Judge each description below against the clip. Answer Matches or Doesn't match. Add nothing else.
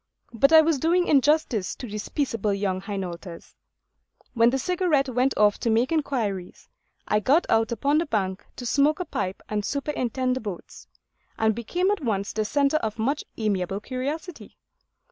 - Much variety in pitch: Matches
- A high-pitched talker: Matches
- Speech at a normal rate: Matches